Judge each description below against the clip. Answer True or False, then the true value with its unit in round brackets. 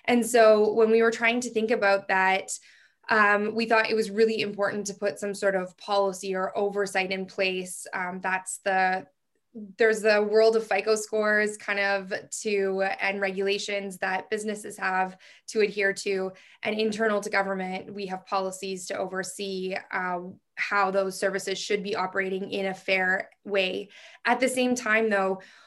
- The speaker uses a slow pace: False (170 wpm)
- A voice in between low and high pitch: False (200 Hz)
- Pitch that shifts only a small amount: True (2.1 semitones)